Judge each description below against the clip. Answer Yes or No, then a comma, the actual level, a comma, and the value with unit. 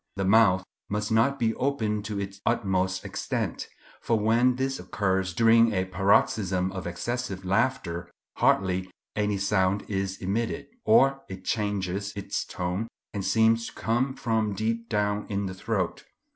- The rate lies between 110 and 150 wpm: Yes, average, 145 wpm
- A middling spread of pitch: Yes, average, 3.2 semitones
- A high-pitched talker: No, low, 100 Hz